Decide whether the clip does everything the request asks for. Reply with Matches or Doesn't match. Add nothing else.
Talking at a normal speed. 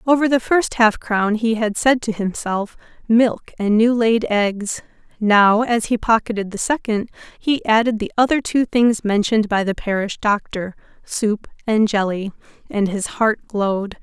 Matches